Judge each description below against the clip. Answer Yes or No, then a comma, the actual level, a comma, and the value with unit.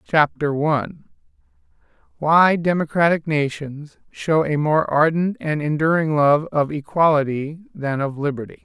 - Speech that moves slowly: Yes, slow, 120 wpm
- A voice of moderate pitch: Yes, medium, 155 Hz